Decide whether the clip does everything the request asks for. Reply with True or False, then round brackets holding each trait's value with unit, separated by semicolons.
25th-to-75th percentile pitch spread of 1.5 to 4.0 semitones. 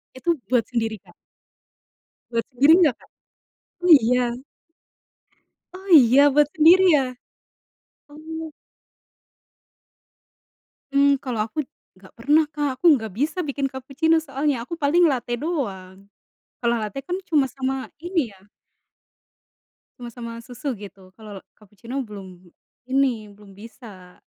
False (5.0 semitones)